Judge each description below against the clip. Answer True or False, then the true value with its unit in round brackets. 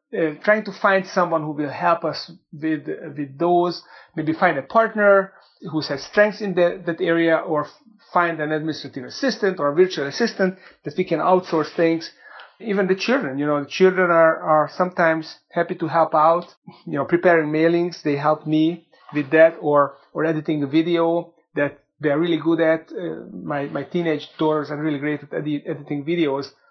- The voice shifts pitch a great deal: False (2.7 semitones)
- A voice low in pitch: False (165 Hz)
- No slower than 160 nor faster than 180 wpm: False (190 wpm)